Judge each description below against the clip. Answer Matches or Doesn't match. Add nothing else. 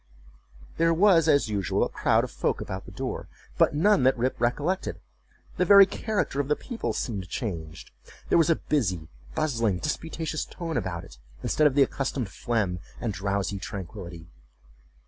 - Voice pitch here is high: Doesn't match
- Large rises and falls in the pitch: Matches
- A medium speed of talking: Matches